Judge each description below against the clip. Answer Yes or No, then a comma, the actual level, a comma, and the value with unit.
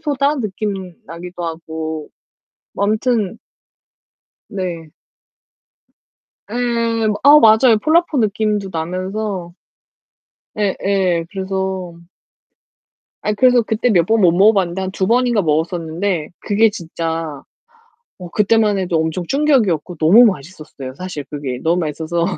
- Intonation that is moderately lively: Yes, average, 4.5 semitones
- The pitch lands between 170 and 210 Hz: Yes, high, 190 Hz